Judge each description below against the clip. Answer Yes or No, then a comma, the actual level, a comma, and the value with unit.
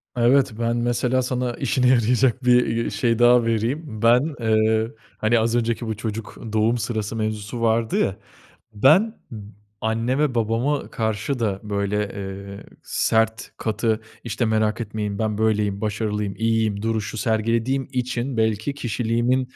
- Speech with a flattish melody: Yes, narrow, 2.1 semitones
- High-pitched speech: No, low, 115 Hz